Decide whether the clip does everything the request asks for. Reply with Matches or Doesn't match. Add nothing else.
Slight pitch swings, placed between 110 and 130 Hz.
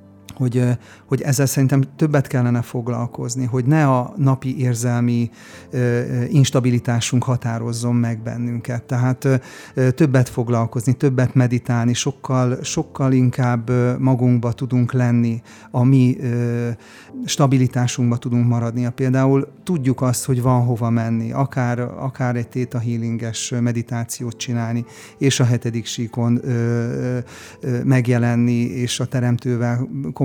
Matches